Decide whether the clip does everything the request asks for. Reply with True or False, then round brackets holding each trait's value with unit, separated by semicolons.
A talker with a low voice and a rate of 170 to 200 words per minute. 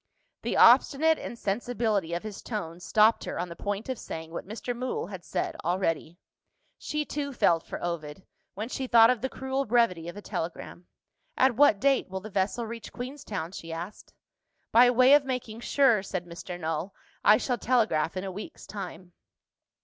False (210 Hz; 180 wpm)